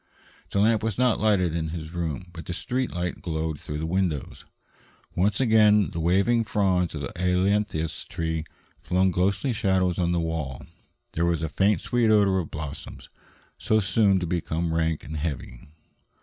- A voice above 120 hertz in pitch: No, very low, 90 Hz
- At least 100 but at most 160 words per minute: No, average, 170 wpm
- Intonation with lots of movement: No, average, 3.7 semitones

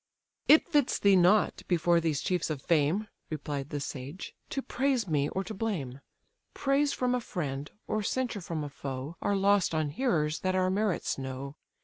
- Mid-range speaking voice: Yes, medium, 175 Hz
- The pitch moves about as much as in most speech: No, wide, 6.5 semitones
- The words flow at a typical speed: Yes, average, 175 wpm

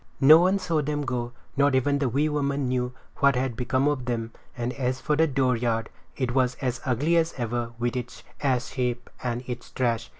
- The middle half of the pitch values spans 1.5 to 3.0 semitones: Yes, average, 2.7 semitones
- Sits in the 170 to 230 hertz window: No, low, 130 Hz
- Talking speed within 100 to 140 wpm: No, average, 200 wpm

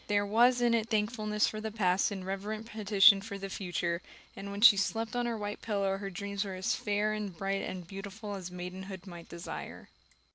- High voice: Yes, high, 200 Hz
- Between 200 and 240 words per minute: Yes, fast, 205 wpm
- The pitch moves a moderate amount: No, narrow, 1.9 semitones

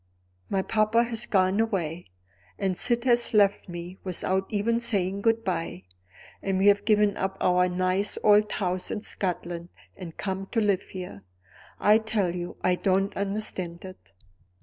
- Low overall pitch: No, high, 195 Hz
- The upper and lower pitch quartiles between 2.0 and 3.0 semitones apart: Yes, narrow, 2.6 semitones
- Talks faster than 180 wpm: No, average, 155 wpm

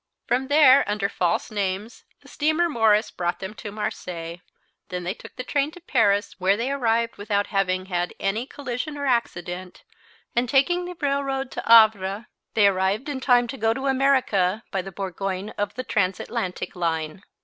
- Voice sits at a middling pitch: No, high, 215 Hz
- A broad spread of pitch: Yes, wide, 5.7 semitones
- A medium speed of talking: Yes, average, 170 wpm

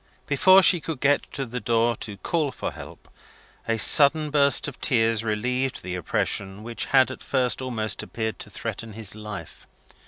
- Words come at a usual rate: Yes, average, 175 wpm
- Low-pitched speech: Yes, low, 120 Hz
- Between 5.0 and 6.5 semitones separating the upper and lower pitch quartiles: No, average, 4.3 semitones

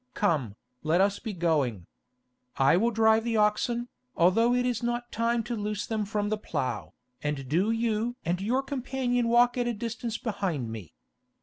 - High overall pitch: Yes, high, 215 Hz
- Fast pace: No, average, 175 wpm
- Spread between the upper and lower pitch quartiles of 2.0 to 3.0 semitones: No, wide, 5.6 semitones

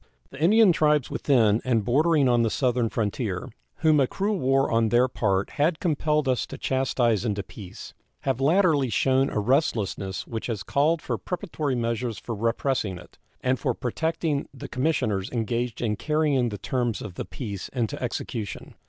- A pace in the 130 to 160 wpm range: No, average, 170 wpm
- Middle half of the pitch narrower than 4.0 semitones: No, average, 4.7 semitones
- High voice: No, low, 125 Hz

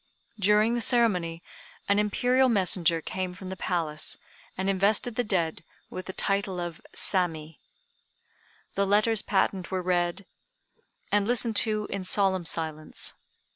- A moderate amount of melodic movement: Yes, average, 3.1 semitones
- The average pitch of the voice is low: No, high, 190 Hz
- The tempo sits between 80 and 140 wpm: Yes, slow, 135 wpm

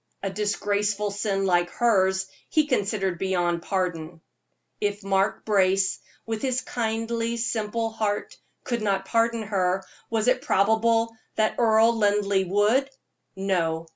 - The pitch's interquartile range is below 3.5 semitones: Yes, average, 2.9 semitones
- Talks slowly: Yes, slow, 125 wpm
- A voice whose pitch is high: Yes, high, 205 Hz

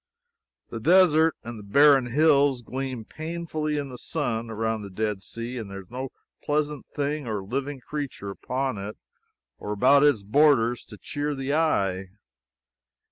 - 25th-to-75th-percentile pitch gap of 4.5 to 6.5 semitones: Yes, average, 4.9 semitones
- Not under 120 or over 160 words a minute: Yes, average, 155 wpm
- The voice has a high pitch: No, low, 130 Hz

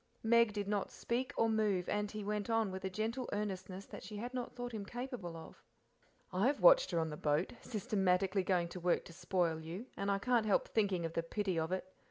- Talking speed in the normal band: No, fast, 225 wpm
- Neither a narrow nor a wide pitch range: Yes, average, 3.8 semitones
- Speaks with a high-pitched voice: Yes, high, 200 Hz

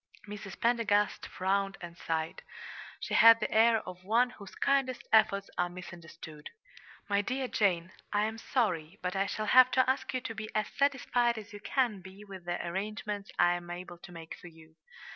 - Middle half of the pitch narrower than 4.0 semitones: No, average, 4.4 semitones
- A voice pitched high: Yes, high, 200 Hz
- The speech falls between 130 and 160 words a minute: No, average, 185 wpm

